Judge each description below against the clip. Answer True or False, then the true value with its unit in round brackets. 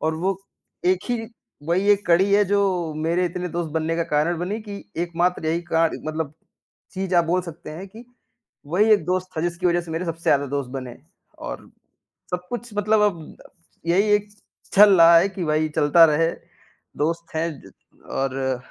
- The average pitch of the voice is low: False (170 Hz)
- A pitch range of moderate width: True (3.0 semitones)